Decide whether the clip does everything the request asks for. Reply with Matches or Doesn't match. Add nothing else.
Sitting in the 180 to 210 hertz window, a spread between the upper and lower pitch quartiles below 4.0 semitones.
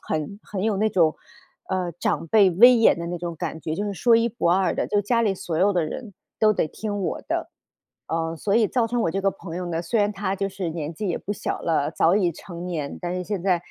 Matches